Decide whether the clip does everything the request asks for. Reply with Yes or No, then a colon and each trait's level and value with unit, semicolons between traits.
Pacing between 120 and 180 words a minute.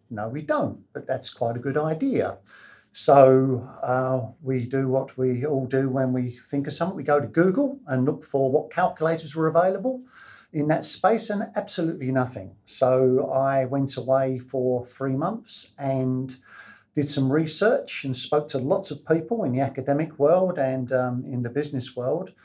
Yes: average, 175 wpm